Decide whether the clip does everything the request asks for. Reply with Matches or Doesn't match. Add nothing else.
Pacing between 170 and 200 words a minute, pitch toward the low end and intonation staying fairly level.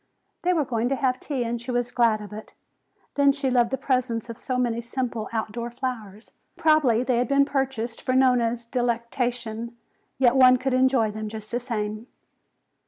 Doesn't match